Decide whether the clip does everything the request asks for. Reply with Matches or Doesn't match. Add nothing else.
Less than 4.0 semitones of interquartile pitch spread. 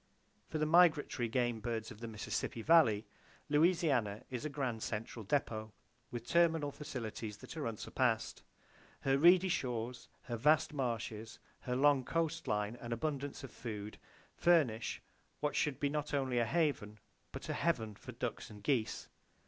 Doesn't match